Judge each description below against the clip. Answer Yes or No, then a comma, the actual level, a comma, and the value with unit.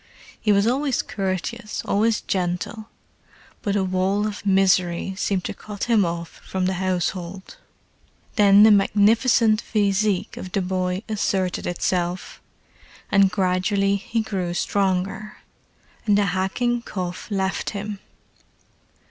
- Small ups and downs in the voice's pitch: Yes, narrow, 2.2 semitones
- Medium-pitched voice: No, high, 195 Hz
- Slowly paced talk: Yes, slow, 120 wpm